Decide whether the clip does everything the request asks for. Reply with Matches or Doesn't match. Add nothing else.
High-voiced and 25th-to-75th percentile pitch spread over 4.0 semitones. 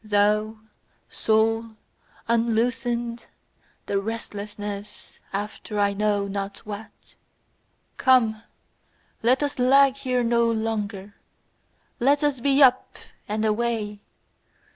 Doesn't match